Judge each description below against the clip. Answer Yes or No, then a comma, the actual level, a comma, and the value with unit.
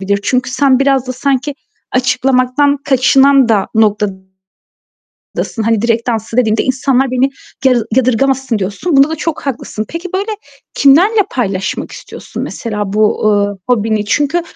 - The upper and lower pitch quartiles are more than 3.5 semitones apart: Yes, average, 4.0 semitones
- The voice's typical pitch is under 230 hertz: No, very high, 255 Hz